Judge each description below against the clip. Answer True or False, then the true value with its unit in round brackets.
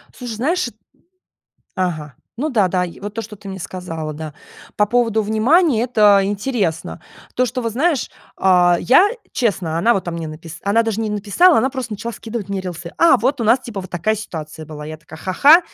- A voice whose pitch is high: True (210 Hz)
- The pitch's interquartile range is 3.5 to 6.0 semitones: True (5.2 semitones)